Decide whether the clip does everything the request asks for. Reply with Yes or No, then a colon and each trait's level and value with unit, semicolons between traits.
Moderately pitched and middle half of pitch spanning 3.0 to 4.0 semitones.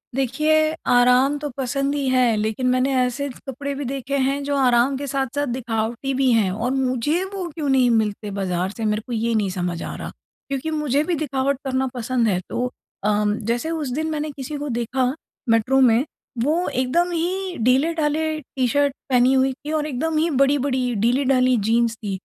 No: very high, 265 Hz; average, 3.3 semitones